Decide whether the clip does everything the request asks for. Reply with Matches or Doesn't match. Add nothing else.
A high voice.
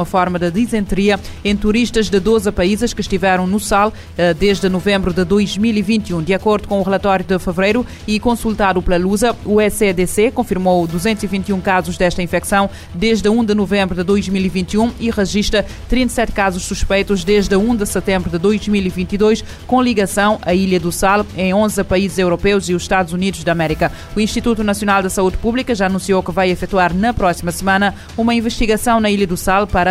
Matches